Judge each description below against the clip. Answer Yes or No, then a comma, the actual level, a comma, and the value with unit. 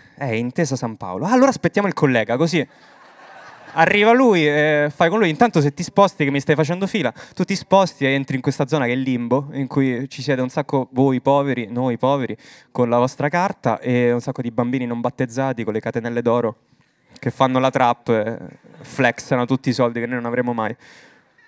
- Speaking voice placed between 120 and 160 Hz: Yes, low, 135 Hz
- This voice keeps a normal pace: No, fast, 220 wpm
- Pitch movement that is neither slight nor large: Yes, average, 4.0 semitones